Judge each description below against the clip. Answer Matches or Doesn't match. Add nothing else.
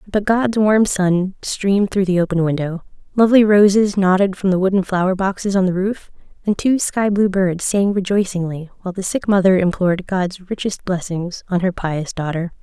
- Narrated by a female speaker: Matches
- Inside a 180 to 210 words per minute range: Matches